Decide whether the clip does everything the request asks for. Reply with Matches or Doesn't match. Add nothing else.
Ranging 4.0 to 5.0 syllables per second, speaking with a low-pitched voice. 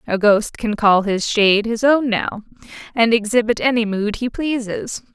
Doesn't match